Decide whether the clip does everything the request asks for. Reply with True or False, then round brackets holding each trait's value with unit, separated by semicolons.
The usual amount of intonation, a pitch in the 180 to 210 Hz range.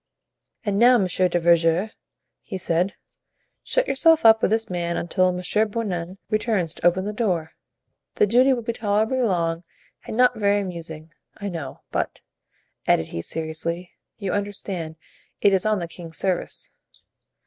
True (4.2 semitones; 190 Hz)